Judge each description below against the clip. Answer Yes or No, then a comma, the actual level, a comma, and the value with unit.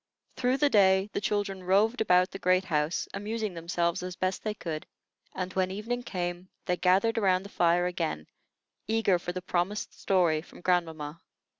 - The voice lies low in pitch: No, medium, 185 Hz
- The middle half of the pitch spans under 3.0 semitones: Yes, narrow, 2.5 semitones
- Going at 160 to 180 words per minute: Yes, average, 170 wpm